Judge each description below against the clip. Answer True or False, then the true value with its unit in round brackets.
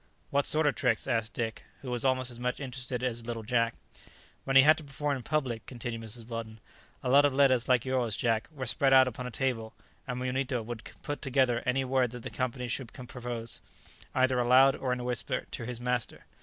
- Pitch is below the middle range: True (125 Hz)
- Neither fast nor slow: False (215 wpm)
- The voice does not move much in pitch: True (2.0 semitones)